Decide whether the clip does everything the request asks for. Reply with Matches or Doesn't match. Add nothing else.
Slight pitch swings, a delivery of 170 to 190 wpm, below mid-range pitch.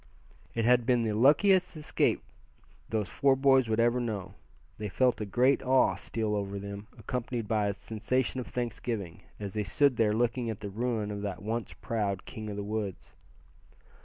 Doesn't match